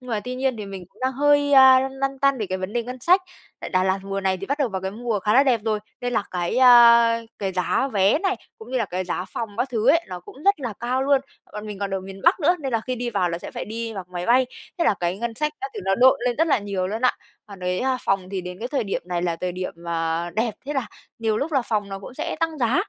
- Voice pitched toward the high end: Yes, high, 225 Hz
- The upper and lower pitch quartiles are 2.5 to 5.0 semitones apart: No, wide, 5.4 semitones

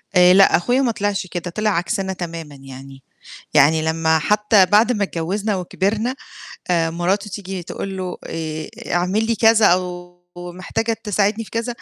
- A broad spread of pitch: No, average, 3.8 semitones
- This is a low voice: No, medium, 185 Hz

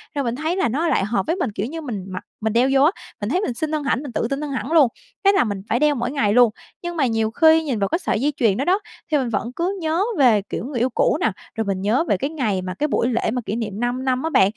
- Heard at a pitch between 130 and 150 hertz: No, very high, 255 Hz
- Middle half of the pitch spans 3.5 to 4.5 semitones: No, average, 5.3 semitones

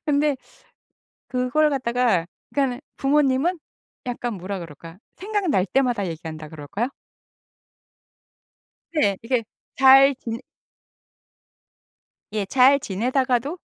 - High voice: Yes, very high, 250 Hz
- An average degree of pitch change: No, wide, 5.8 semitones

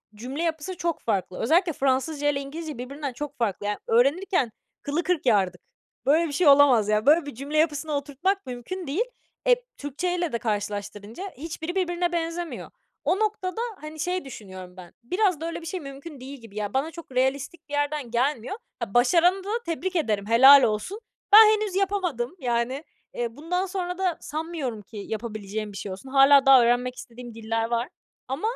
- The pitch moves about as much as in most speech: No, wide, 6.3 semitones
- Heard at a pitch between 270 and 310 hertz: Yes, very high, 285 Hz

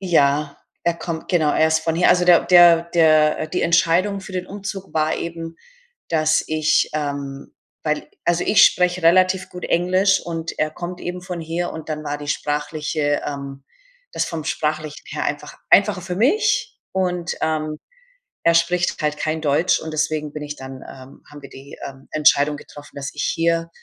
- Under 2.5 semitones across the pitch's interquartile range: No, average, 2.8 semitones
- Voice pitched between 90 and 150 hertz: No, medium, 160 Hz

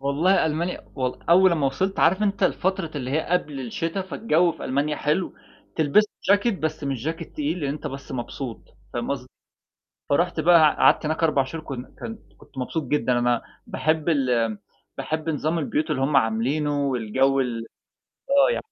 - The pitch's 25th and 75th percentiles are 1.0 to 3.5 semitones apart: No, average, 3.9 semitones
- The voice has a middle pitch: Yes, medium, 150 Hz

